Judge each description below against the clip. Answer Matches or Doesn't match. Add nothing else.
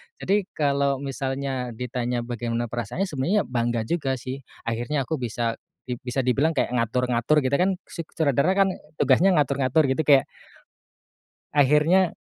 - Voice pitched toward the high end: Doesn't match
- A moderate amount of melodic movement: Matches